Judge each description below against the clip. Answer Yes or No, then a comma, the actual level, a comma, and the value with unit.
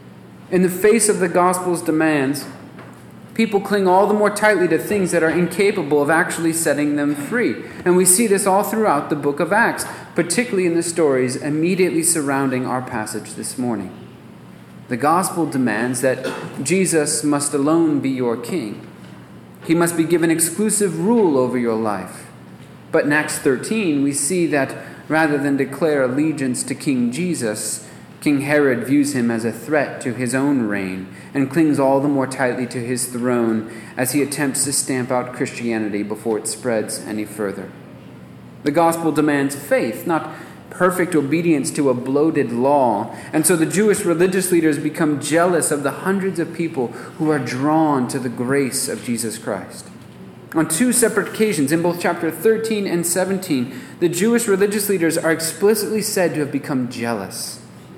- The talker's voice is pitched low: No, medium, 150 Hz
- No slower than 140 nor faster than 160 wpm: No, average, 170 wpm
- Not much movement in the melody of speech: No, wide, 5.5 semitones